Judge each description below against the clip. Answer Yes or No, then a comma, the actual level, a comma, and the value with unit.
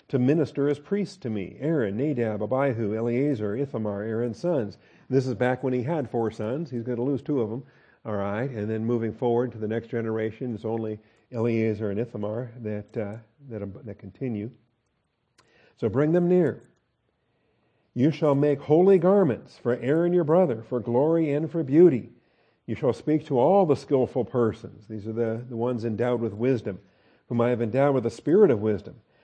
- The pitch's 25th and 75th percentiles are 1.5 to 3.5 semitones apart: No, average, 4.2 semitones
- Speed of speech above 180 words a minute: Yes, average, 190 wpm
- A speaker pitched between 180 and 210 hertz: No, low, 120 Hz